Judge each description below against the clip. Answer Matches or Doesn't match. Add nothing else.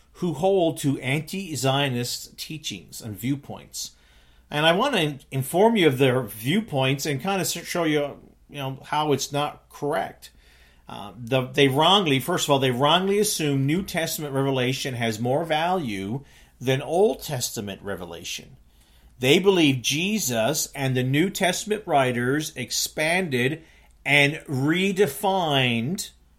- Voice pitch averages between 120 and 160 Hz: Matches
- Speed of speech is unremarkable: Doesn't match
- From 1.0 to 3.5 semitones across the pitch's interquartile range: Doesn't match